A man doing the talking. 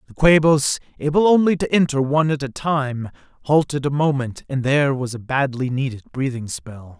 Yes: male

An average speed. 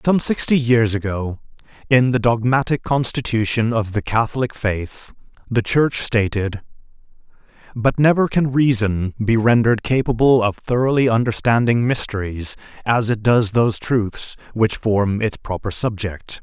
No: slow, 130 wpm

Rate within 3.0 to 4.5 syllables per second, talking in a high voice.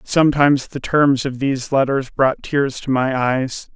No: 4.4 syllables/s; low, 135 Hz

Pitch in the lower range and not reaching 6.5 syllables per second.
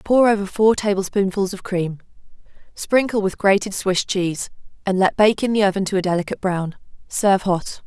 No: high, 195 Hz; 5.5 syllables/s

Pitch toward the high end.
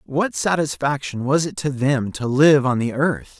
No: medium, 140 Hz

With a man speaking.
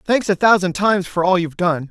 Yes: male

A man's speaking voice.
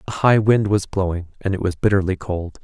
Yes: male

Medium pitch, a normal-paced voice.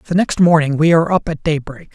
No: medium, 160 Hz; fast, 245 wpm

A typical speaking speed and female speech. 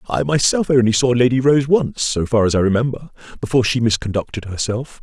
No: average, 190 wpm; male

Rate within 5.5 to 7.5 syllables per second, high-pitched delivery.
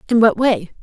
Yes: 5.7 syllables/s; high, 215 Hz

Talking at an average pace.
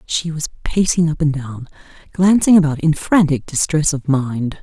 Yes: average, 170 wpm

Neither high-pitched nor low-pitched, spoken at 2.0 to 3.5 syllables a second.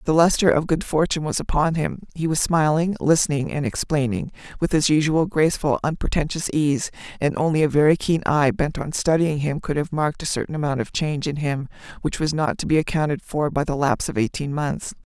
No: medium, 150 Hz; 5.8 syllables/s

